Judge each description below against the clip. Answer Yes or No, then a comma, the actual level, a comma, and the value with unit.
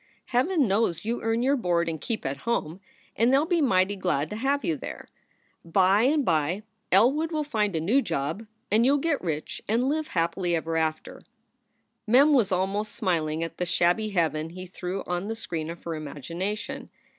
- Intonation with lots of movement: Yes, wide, 6.2 semitones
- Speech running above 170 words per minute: Yes, average, 195 wpm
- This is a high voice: Yes, high, 195 Hz